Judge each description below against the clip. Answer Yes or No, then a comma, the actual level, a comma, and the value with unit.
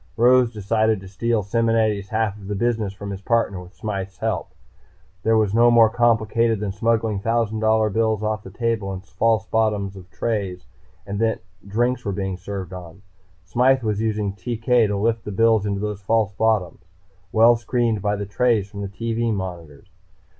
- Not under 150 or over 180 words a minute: Yes, average, 175 wpm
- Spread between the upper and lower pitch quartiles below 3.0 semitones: Yes, narrow, 2.5 semitones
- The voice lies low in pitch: Yes, low, 110 Hz